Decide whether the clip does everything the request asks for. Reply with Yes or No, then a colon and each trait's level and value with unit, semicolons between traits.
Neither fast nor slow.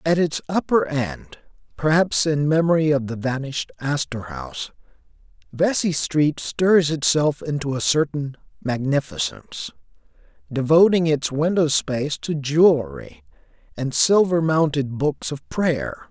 No: slow, 120 wpm